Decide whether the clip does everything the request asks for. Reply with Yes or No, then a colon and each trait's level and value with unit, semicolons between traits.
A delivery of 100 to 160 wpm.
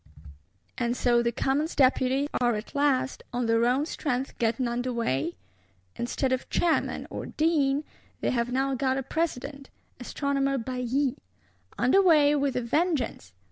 Yes: average, 145 wpm